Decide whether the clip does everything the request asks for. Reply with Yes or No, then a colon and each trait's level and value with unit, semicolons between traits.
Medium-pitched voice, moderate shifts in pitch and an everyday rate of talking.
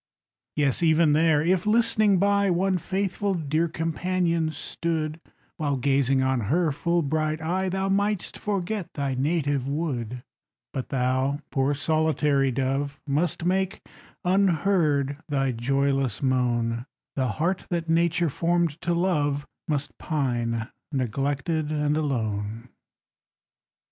No: medium, 150 Hz; average, 4.2 semitones; slow, 120 wpm